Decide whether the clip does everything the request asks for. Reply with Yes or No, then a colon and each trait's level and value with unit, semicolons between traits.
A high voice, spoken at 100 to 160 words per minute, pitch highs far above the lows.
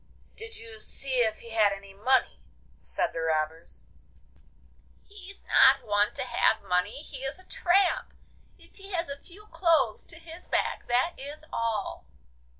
Yes: very high, 270 Hz; average, 155 wpm; wide, 9.0 semitones